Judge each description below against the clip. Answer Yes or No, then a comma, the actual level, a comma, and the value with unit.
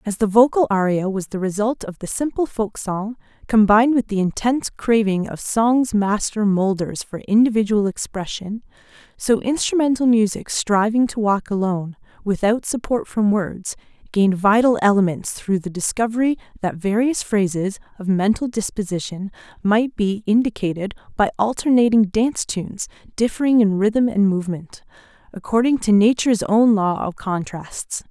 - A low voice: No, high, 210 Hz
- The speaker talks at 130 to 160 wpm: Yes, average, 140 wpm